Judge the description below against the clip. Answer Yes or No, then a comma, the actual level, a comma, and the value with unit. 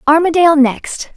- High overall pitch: Yes, very high, 305 Hz